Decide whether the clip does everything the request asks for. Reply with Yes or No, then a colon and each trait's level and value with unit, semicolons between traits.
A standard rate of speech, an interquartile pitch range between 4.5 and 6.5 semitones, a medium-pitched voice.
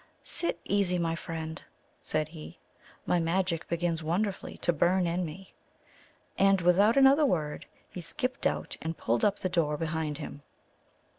No: average, 150 wpm; average, 3.1 semitones; medium, 170 Hz